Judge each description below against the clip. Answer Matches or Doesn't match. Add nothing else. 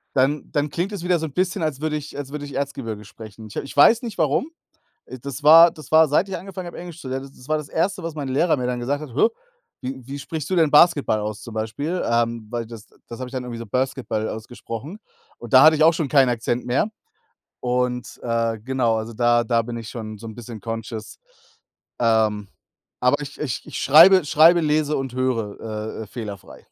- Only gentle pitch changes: Doesn't match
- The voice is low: Matches